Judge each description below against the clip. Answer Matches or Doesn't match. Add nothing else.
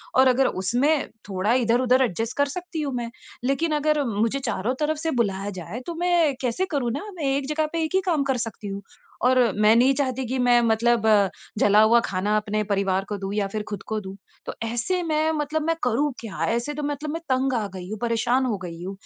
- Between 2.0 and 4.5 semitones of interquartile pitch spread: Doesn't match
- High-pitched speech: Matches